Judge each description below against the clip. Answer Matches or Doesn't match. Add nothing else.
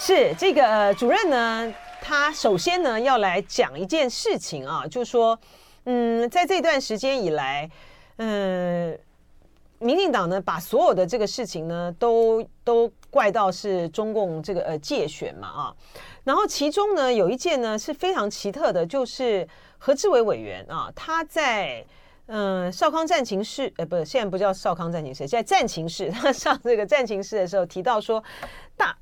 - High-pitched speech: Matches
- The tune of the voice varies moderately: Doesn't match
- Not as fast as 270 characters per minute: Matches